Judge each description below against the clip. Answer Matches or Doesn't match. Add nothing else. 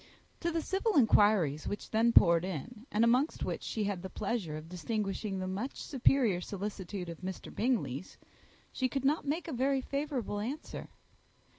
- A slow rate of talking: Doesn't match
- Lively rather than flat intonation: Matches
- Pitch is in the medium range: Doesn't match